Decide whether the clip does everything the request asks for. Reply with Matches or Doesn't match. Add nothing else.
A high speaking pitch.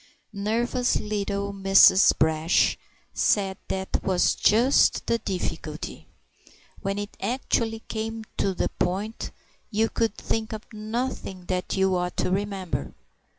Matches